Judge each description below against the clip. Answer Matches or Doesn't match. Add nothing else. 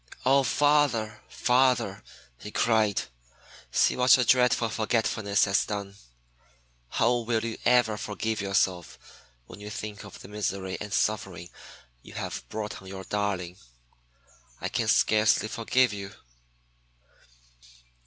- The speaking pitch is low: Matches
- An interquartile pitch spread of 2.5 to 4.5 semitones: Matches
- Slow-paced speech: Matches